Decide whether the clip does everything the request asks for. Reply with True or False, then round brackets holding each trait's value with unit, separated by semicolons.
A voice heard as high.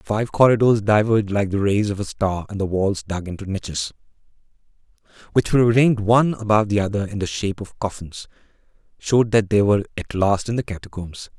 False (105 Hz)